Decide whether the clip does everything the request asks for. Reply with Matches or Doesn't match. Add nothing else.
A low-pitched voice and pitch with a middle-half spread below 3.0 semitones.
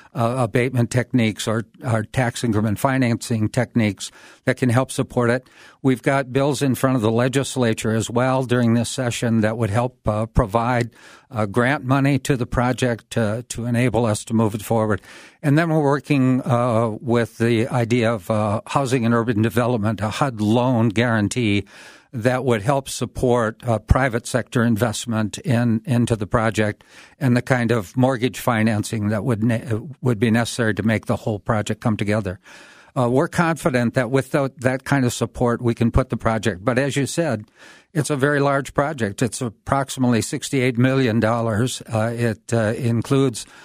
Matches